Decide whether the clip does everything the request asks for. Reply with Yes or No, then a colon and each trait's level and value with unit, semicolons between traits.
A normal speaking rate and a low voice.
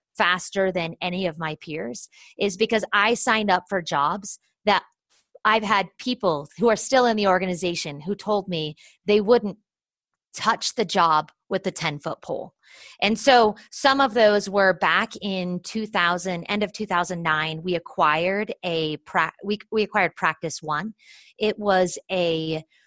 No: average, 150 wpm; high, 190 Hz